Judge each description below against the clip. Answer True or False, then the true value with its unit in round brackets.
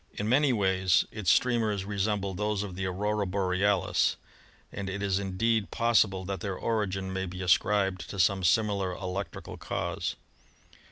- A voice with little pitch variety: True (1.9 semitones)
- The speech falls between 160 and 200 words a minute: False (150 wpm)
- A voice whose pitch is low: True (100 Hz)